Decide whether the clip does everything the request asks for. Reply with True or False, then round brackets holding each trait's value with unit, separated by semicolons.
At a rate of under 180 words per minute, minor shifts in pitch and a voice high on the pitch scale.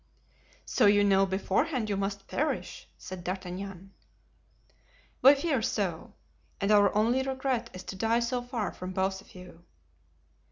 False (145 wpm; 4.1 semitones; 200 Hz)